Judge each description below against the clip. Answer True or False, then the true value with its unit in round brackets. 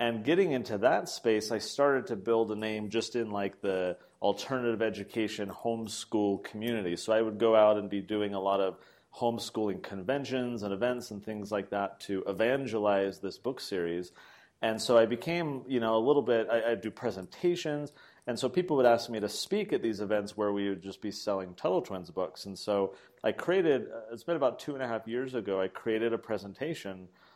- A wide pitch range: False (2.8 semitones)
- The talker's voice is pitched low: True (110 Hz)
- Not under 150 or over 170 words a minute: False (205 wpm)